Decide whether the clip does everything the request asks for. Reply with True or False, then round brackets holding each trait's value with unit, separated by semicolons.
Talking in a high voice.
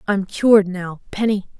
True (200 Hz)